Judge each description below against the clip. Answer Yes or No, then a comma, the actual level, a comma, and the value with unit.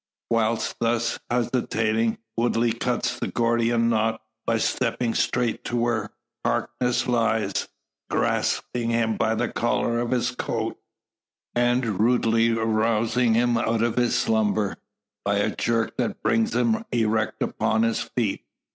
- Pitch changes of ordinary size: No, narrow, 1.3 semitones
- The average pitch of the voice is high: No, low, 115 Hz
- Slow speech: Yes, slow, 125 wpm